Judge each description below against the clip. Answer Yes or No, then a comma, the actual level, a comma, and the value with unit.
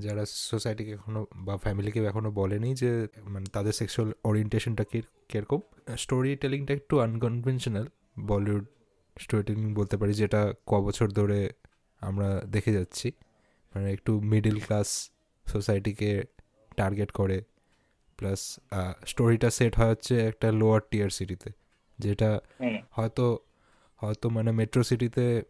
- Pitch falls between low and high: No, low, 110 Hz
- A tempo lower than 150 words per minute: Yes, fast, 120 wpm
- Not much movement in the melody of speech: Yes, narrow, 2.1 semitones